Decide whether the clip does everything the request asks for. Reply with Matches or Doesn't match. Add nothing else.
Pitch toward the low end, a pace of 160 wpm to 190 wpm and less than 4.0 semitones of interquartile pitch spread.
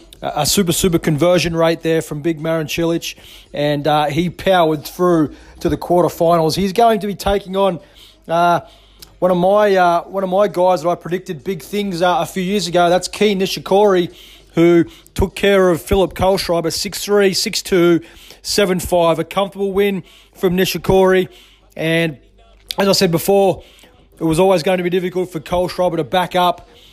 Doesn't match